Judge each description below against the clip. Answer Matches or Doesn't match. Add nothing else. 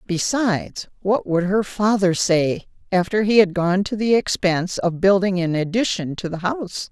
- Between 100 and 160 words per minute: Doesn't match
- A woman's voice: Matches